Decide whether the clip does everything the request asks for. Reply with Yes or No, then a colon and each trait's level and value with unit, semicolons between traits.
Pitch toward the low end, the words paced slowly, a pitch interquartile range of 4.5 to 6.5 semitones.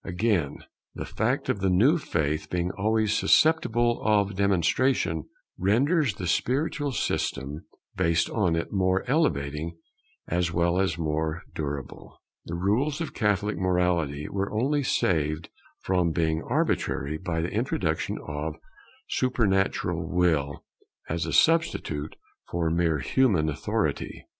Yes: very low, 90 Hz; slow, 125 wpm; average, 5.2 semitones